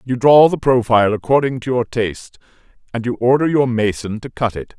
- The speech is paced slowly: No, average, 200 wpm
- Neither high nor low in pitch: No, low, 120 Hz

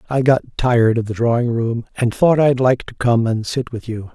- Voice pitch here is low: Yes, low, 120 Hz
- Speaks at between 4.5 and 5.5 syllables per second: Yes, 5.1 syllables/s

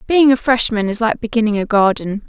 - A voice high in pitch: Yes, high, 225 Hz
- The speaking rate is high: Yes, fast, 210 wpm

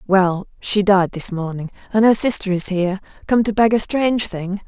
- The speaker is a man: No, female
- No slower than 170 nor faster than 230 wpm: Yes, average, 190 wpm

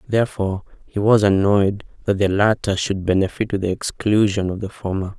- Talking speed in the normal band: Yes, average, 175 wpm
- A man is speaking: Yes, male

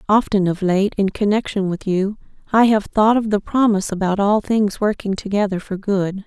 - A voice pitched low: No, high, 200 Hz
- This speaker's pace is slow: No, average, 190 wpm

